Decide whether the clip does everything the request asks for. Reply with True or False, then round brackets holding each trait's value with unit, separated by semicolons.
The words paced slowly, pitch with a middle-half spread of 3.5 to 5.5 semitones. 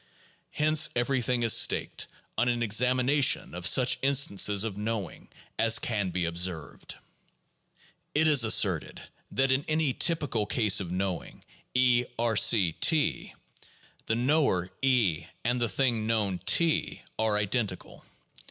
True (125 wpm; 4.7 semitones)